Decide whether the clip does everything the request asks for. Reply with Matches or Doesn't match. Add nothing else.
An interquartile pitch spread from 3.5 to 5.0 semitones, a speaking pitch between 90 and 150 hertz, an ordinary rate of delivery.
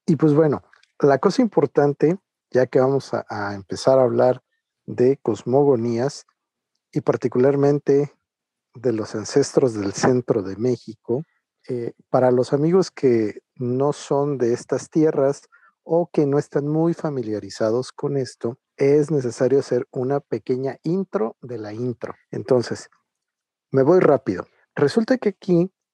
Matches